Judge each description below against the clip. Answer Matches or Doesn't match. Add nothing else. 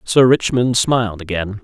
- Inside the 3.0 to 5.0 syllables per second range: Matches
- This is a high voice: Doesn't match